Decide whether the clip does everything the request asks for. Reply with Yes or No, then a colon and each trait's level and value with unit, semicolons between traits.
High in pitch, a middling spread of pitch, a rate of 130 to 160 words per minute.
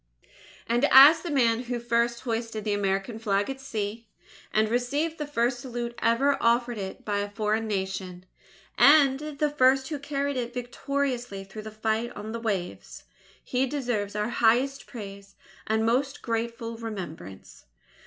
Yes: high, 235 Hz; average, 3.8 semitones; average, 155 wpm